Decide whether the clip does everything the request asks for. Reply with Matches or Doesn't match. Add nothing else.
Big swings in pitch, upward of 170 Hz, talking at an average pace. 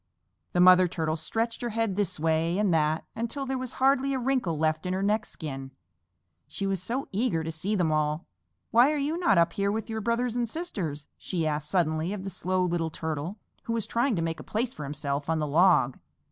Doesn't match